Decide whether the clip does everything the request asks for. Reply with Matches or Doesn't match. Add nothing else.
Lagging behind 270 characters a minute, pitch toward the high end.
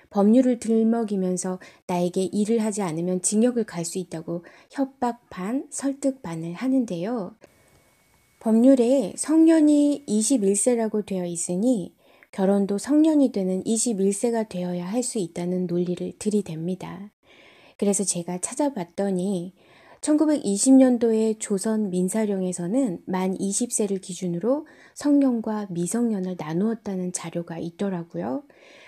Matches